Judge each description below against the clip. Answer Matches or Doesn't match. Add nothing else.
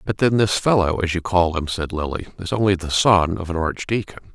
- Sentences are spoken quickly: Matches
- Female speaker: Doesn't match